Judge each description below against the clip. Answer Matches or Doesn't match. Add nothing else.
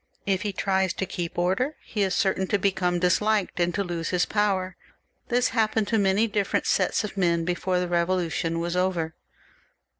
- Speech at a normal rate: Matches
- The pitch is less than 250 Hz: Matches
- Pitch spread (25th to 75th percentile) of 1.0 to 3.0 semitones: Matches